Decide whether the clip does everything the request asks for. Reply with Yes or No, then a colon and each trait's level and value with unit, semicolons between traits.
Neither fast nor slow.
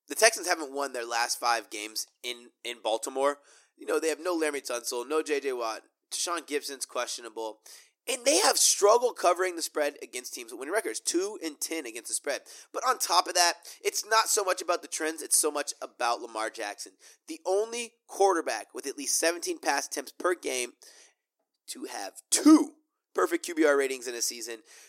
Yes: average, 195 wpm